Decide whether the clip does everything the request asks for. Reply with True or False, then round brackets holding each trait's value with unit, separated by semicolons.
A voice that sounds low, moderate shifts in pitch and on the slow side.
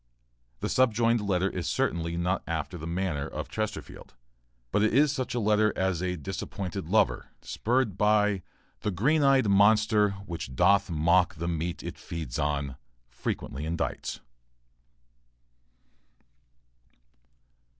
True (95 Hz; 4.2 semitones; 125 wpm)